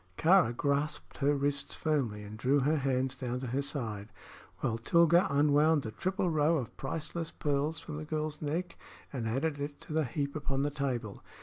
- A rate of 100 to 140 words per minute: No, average, 185 wpm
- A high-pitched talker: No, medium, 145 Hz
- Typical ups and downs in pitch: Yes, average, 3.1 semitones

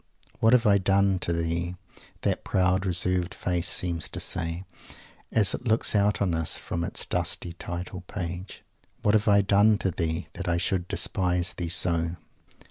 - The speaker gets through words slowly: No, average, 170 wpm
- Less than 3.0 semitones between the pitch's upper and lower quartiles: Yes, narrow, 2.5 semitones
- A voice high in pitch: No, very low, 90 Hz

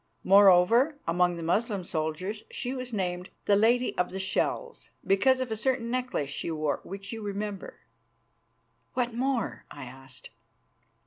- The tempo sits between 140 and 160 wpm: Yes, average, 150 wpm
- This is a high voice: Yes, high, 200 Hz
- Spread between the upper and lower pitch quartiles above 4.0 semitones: Yes, average, 5.3 semitones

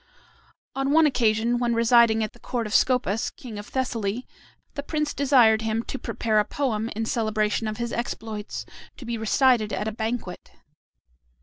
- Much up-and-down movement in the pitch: No, narrow, 2.5 semitones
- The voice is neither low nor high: No, high, 230 Hz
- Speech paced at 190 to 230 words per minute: No, average, 170 wpm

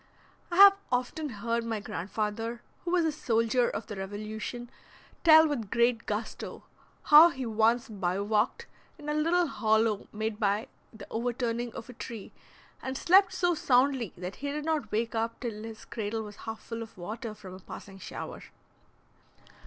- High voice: Yes, high, 230 Hz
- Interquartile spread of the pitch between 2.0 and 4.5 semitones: Yes, average, 3.8 semitones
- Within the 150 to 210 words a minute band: Yes, average, 170 wpm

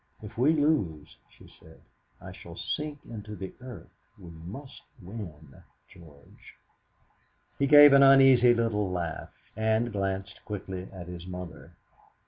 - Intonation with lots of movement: Yes, wide, 6.1 semitones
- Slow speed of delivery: Yes, slow, 130 wpm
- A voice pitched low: Yes, low, 105 Hz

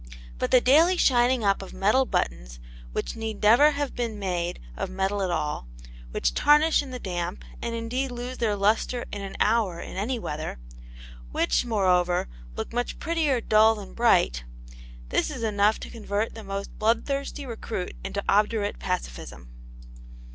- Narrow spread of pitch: No, average, 4.4 semitones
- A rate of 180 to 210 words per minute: No, average, 160 wpm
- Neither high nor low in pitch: No, high, 215 Hz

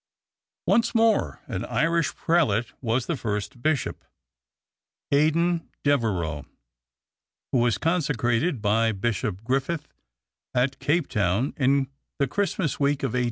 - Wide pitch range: Yes, wide, 5.7 semitones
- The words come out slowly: Yes, slow, 115 wpm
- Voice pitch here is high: No, low, 135 Hz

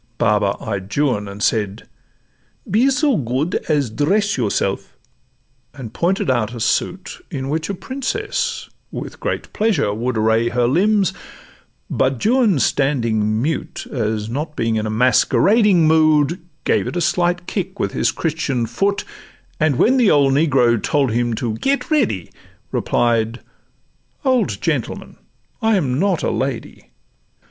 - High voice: No, medium, 140 Hz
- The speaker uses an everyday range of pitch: No, wide, 8.5 semitones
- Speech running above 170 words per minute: No, average, 140 wpm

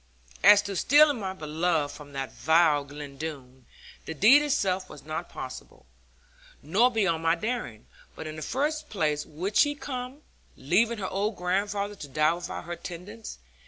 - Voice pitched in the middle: Yes, medium, 180 Hz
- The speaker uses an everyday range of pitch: No, wide, 6.0 semitones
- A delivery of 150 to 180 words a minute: Yes, average, 160 wpm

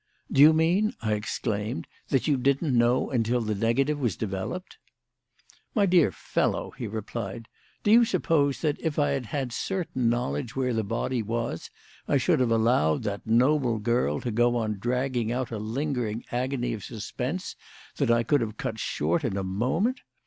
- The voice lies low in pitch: Yes, low, 120 Hz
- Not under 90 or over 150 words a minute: No, average, 175 wpm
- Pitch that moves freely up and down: No, average, 4.2 semitones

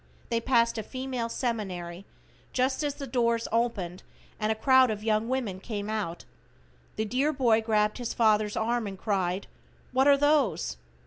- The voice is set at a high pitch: Yes, high, 230 Hz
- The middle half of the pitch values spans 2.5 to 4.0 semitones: Yes, average, 3.3 semitones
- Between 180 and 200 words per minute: No, average, 165 wpm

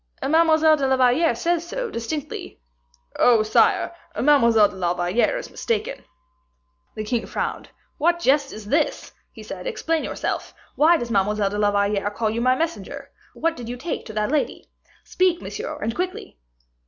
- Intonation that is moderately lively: No, wide, 7.3 semitones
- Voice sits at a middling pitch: No, very high, 260 Hz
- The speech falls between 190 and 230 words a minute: No, average, 165 wpm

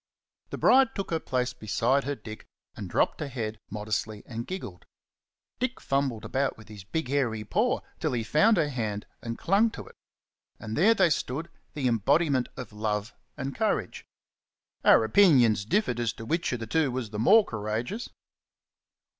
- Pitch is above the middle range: No, low, 125 Hz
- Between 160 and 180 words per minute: Yes, average, 170 wpm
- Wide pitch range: Yes, wide, 6.6 semitones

